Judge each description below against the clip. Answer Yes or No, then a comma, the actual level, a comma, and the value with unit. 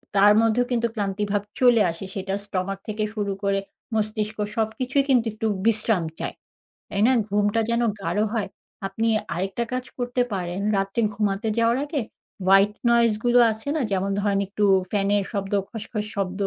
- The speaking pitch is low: No, high, 210 Hz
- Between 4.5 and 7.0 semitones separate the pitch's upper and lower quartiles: No, narrow, 2.6 semitones